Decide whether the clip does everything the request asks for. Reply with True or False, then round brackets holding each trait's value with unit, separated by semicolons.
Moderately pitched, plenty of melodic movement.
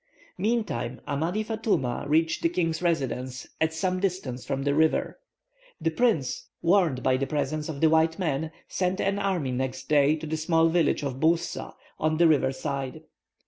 False (160 Hz; 3.9 semitones)